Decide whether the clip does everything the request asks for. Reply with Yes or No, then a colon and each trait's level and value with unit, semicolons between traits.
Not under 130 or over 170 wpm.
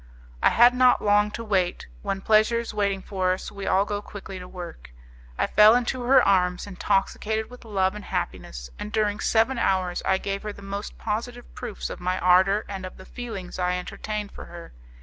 No: average, 200 wpm